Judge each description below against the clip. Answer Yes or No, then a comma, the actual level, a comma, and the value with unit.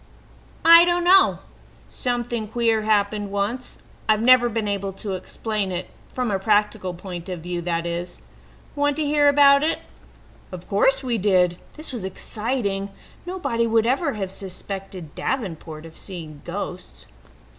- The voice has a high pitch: Yes, high, 210 Hz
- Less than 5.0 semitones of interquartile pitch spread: No, average, 5.3 semitones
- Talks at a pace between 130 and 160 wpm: Yes, average, 145 wpm